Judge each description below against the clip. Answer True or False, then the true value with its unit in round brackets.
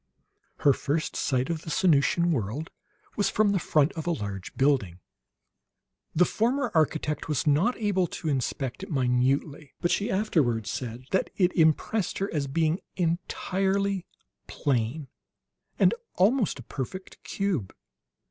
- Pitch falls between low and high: True (160 Hz)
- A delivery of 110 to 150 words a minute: True (140 wpm)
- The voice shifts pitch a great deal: True (5.9 semitones)